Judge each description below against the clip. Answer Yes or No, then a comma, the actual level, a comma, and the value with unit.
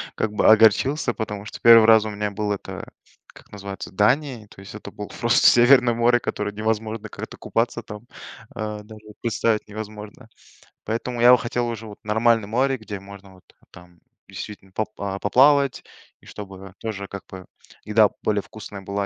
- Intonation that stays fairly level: Yes, narrow, 2.3 semitones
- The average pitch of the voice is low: Yes, low, 110 Hz